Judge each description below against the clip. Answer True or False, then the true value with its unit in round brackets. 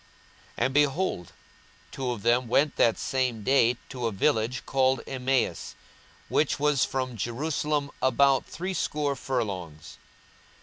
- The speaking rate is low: True (125 wpm)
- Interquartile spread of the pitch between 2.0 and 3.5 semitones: True (3.0 semitones)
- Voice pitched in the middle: False (130 Hz)